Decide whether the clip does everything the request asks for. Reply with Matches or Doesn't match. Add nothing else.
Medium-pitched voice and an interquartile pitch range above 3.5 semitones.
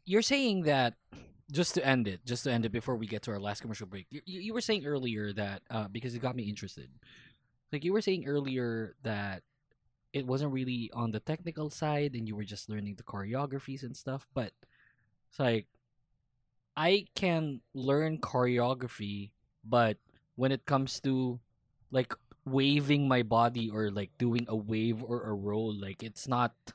Doesn't match